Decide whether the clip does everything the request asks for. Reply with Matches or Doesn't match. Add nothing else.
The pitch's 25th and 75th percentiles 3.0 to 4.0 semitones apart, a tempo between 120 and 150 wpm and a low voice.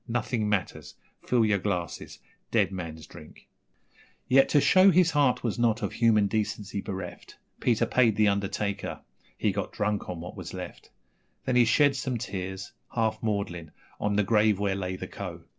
Doesn't match